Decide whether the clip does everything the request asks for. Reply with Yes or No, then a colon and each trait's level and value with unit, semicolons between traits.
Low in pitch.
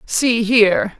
No: high, 220 Hz